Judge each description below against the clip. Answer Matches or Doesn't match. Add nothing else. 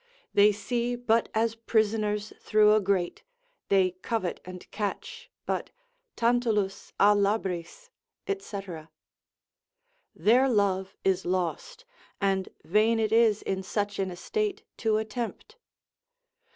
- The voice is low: Doesn't match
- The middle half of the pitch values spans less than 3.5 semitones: Matches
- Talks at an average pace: Doesn't match